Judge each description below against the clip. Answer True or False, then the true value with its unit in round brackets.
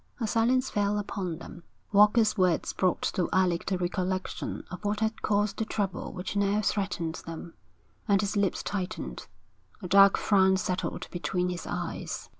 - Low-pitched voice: False (195 Hz)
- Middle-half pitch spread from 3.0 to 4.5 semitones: False (2.4 semitones)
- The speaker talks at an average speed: True (160 wpm)